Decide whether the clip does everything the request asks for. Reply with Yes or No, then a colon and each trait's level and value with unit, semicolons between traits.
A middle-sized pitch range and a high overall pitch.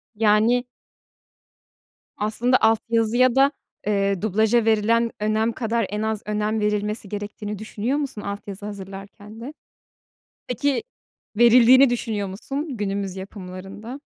No: narrow, 2.3 semitones; high, 215 Hz